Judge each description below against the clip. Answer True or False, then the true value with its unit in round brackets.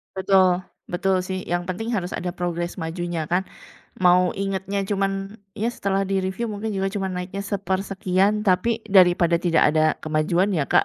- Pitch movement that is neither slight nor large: False (1.9 semitones)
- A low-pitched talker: False (190 Hz)